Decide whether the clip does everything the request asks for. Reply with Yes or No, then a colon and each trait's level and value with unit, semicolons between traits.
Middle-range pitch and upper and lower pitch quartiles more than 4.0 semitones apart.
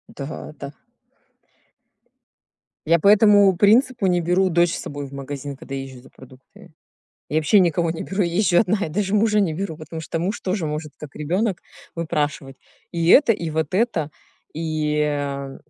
Yes: medium, 165 Hz; average, 4.6 semitones